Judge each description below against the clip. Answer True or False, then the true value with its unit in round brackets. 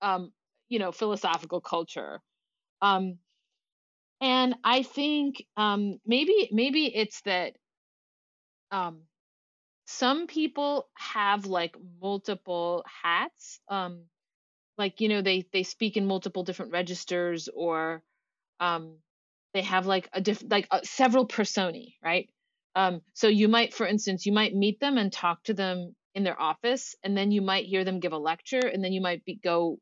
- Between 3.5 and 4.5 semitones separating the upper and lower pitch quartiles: True (4.1 semitones)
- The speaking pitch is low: False (195 Hz)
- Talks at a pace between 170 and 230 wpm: False (155 wpm)